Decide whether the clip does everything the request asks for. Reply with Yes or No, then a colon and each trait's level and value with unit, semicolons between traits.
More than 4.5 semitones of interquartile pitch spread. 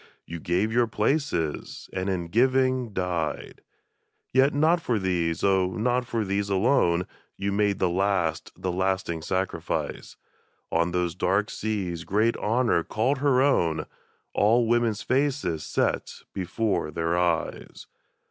Yes: average, 5.2 semitones